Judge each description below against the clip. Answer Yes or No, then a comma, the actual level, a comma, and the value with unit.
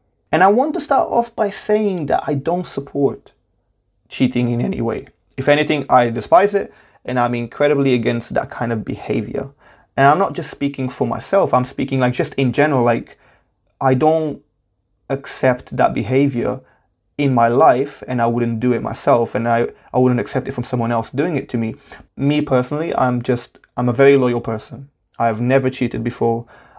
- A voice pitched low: Yes, low, 130 Hz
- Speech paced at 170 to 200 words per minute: Yes, average, 190 wpm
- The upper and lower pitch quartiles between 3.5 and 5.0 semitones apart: No, average, 3.0 semitones